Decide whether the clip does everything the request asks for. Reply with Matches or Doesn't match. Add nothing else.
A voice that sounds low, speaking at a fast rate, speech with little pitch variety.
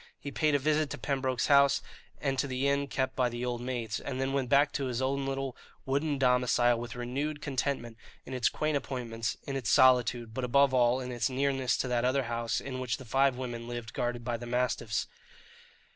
Matches